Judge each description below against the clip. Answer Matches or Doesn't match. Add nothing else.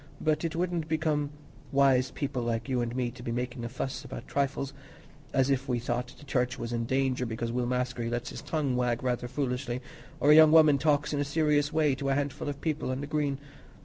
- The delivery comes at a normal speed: Doesn't match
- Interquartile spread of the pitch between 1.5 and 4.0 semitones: Matches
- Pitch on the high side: Doesn't match